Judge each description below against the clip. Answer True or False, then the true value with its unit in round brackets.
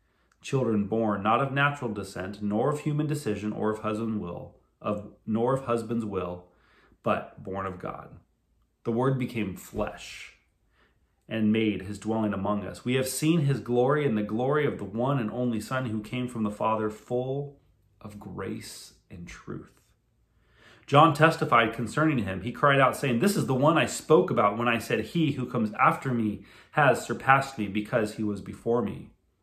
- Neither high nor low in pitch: False (115 Hz)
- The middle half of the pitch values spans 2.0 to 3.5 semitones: False (3.9 semitones)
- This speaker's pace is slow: False (180 wpm)